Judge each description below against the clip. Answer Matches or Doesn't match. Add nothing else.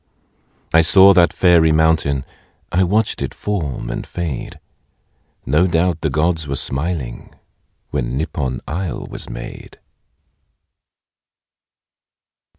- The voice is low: Matches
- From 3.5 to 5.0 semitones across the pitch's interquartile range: Matches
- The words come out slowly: Matches